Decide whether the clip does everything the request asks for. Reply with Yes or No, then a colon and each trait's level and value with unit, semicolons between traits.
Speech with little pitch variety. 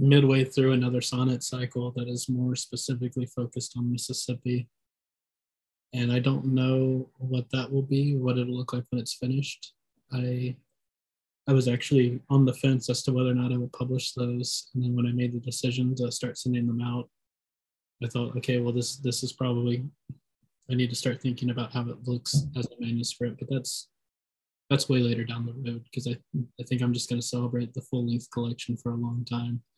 Yes: narrow, 1.2 semitones